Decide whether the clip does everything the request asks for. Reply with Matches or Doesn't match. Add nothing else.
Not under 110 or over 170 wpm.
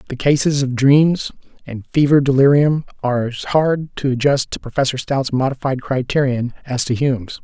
Matches